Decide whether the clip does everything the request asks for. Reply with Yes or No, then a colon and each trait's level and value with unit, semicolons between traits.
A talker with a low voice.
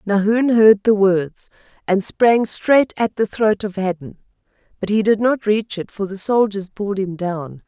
No: high, 205 Hz